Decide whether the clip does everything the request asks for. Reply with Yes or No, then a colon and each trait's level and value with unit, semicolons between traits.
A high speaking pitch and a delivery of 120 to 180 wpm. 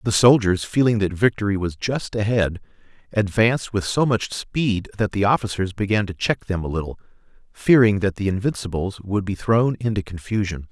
No: low, 105 Hz; average, 175 wpm